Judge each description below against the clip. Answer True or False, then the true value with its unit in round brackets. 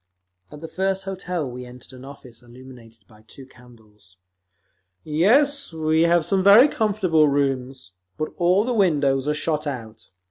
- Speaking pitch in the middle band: True (150 Hz)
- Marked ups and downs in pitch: True (6.6 semitones)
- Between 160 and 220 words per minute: False (150 wpm)